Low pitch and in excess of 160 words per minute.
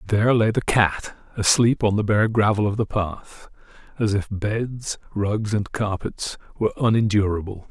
No: low, 105 Hz; average, 155 wpm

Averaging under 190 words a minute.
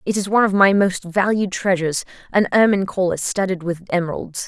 Yes: average, 175 wpm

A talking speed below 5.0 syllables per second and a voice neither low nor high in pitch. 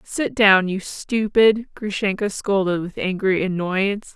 No: 4.0 syllables/s; high, 200 Hz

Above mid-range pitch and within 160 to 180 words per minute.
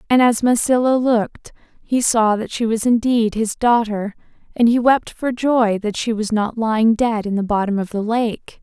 No: high, 225 Hz; average, 200 wpm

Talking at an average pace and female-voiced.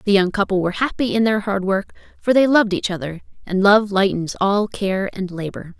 No: fast, 220 wpm; female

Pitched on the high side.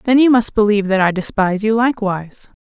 Yes: high, 210 Hz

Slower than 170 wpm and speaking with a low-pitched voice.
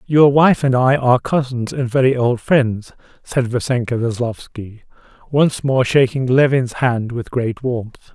Yes: average, 155 wpm; low, 125 Hz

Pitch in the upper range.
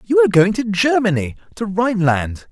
No: medium, 180 Hz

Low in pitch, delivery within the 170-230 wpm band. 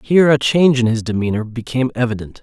Yes: low, 125 Hz; average, 200 wpm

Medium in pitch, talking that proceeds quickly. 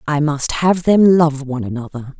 No: medium, 150 Hz; average, 190 wpm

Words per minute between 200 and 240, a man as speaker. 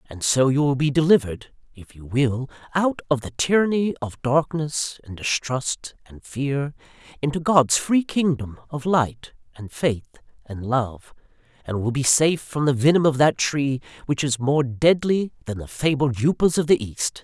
No: average, 175 wpm; male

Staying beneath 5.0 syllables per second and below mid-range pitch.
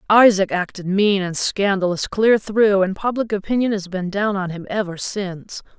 No: 4.8 syllables/s; high, 195 Hz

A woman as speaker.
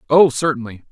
No: male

